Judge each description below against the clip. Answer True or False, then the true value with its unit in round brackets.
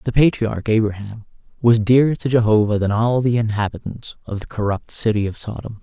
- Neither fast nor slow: True (175 wpm)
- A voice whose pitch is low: True (110 Hz)